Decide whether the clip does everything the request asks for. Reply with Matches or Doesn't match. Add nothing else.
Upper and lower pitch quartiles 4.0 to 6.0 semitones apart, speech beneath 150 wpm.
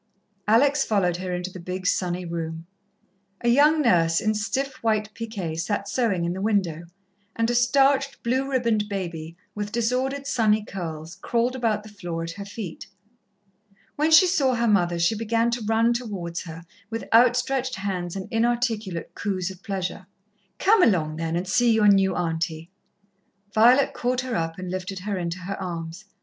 Doesn't match